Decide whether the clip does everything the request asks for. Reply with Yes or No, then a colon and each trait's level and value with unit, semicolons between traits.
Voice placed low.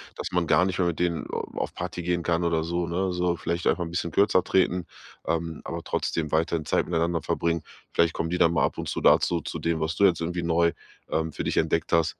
Yes: very low, 85 Hz